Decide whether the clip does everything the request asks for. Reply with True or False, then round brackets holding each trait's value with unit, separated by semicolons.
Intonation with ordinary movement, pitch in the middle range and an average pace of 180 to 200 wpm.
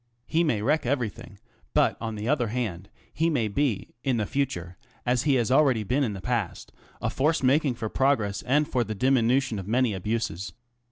False (4.2 semitones; 120 Hz; 190 wpm)